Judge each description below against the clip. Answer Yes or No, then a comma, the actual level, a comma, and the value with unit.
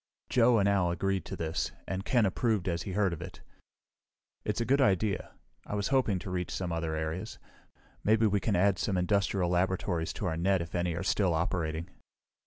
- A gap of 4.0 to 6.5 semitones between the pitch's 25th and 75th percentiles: No, average, 2.9 semitones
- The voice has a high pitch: No, very low, 95 Hz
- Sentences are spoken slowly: No, average, 200 wpm